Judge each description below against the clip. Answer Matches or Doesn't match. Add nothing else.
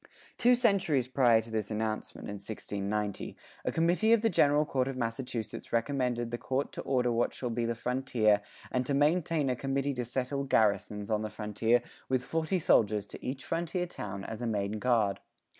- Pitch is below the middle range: Matches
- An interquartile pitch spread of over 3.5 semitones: Matches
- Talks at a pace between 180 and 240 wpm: Matches